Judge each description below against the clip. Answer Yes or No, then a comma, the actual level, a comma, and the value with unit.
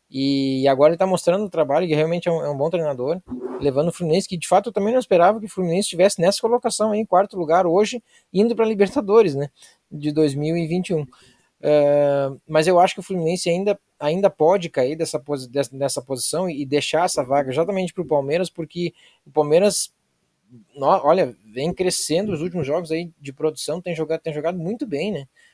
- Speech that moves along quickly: Yes, fast, 195 wpm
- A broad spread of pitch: No, average, 4.2 semitones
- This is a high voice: No, medium, 170 Hz